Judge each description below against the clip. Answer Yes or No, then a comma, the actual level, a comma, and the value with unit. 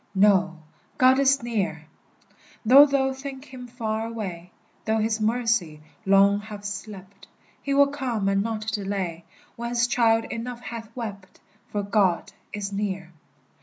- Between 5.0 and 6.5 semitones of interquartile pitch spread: No, average, 3.5 semitones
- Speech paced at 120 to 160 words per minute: Yes, average, 140 wpm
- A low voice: No, high, 220 Hz